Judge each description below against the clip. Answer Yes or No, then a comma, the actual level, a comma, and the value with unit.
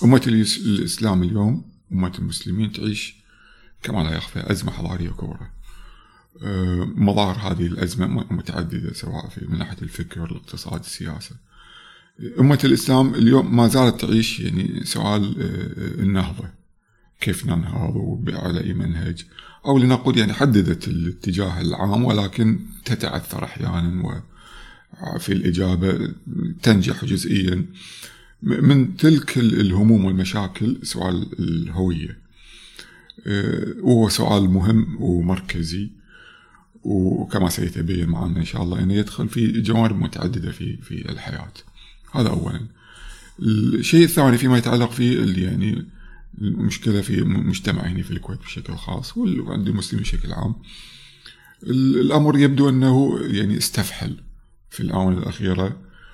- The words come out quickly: No, average, 110 wpm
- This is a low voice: Yes, low, 100 Hz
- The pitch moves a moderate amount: Yes, average, 4.4 semitones